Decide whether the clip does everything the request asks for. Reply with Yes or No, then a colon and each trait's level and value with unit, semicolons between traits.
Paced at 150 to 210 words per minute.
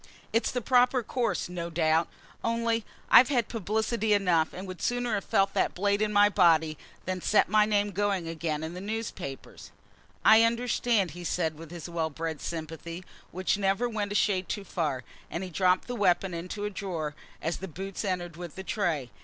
Yes: average, 190 wpm